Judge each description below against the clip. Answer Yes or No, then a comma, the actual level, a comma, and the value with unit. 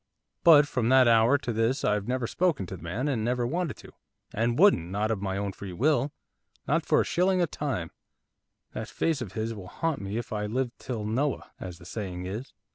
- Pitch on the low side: Yes, low, 115 Hz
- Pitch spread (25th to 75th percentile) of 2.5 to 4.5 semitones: No, wide, 5.4 semitones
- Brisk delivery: Yes, fast, 215 wpm